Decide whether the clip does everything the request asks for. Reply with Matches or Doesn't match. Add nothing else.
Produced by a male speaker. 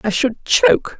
Doesn't match